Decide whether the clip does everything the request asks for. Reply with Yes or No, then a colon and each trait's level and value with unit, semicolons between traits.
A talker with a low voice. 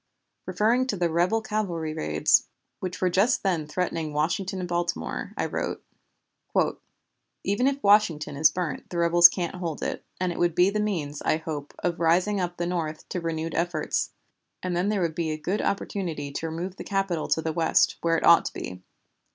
No: medium, 175 Hz